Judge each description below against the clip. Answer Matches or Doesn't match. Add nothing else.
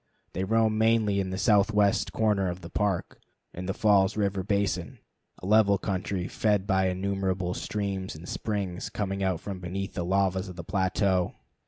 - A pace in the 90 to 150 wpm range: Doesn't match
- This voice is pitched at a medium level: Doesn't match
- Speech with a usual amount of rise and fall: Doesn't match